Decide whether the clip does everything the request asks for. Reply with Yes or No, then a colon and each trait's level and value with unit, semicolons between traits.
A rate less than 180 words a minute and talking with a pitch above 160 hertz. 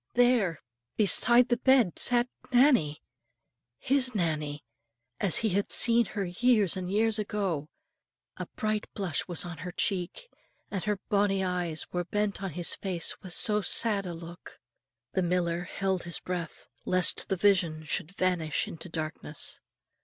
Yes: average, 150 wpm; high, 190 Hz